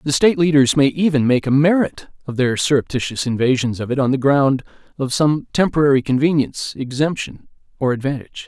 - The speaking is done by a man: Yes, male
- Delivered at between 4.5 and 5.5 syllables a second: No, 5.9 syllables/s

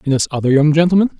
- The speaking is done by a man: Yes, male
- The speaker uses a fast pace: Yes, fast, 250 wpm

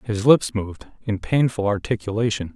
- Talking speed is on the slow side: Yes, slow, 115 wpm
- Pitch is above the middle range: No, low, 110 Hz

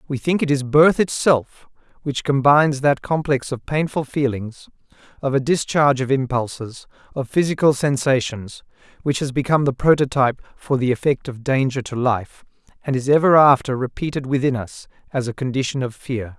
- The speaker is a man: Yes, male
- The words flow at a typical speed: Yes, average, 165 wpm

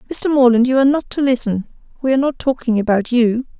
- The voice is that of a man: No, female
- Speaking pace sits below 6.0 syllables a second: No, 6.5 syllables/s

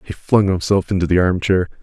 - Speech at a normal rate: Yes, average, 195 wpm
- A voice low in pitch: Yes, very low, 90 Hz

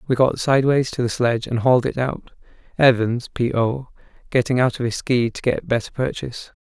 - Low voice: Yes, low, 125 Hz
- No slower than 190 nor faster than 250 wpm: Yes, average, 200 wpm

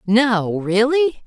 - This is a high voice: Yes, high, 230 Hz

